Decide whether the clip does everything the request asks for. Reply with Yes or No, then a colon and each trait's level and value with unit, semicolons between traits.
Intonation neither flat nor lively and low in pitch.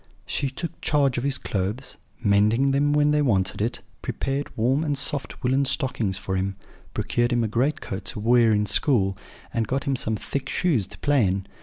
Yes: average, 4.9 semitones; low, 125 Hz